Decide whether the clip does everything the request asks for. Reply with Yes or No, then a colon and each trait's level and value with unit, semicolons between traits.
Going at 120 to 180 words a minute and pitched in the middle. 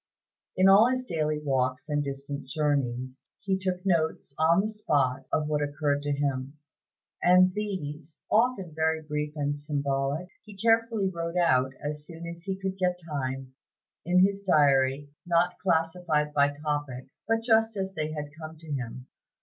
Yes: average, 160 wpm; medium, 155 Hz